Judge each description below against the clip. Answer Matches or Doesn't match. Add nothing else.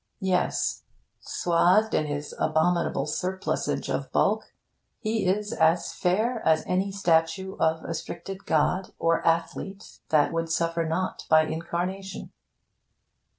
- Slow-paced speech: Matches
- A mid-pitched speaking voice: Matches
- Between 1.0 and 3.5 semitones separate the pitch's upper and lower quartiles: Matches